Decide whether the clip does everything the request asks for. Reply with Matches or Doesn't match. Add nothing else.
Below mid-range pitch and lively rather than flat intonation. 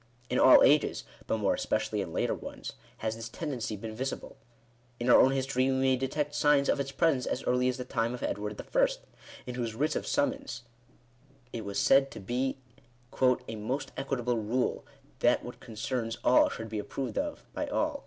Doesn't match